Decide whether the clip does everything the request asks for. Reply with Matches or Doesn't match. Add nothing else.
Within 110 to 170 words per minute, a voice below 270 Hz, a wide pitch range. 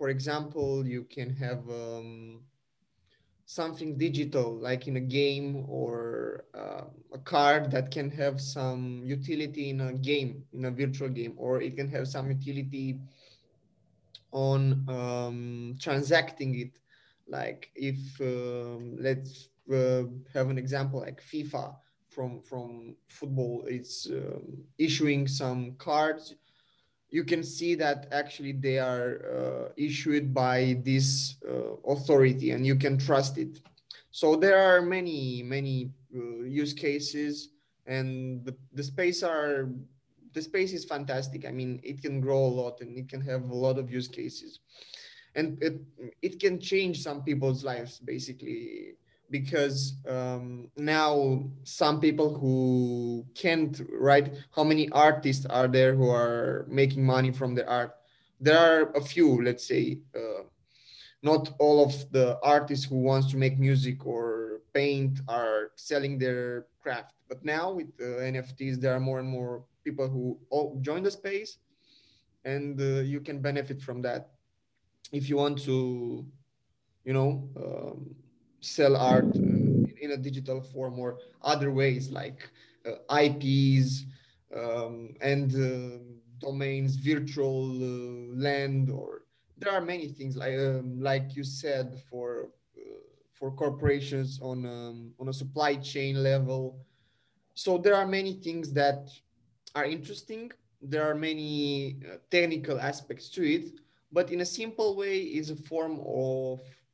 Doesn't match